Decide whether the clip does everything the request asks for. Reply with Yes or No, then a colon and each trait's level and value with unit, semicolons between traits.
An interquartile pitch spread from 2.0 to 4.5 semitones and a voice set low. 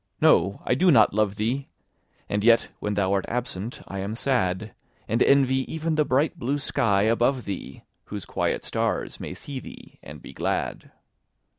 No: average, 5.0 semitones; low, 115 Hz